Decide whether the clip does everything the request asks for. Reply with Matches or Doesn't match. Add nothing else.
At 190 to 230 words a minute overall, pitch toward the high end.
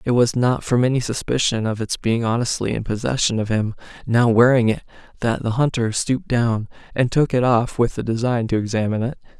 Doesn't match